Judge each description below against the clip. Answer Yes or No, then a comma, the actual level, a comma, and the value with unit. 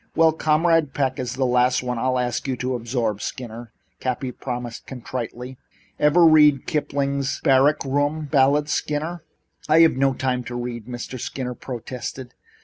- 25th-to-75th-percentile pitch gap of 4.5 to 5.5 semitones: No, average, 3.0 semitones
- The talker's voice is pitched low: Yes, low, 130 Hz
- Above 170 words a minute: No, average, 150 wpm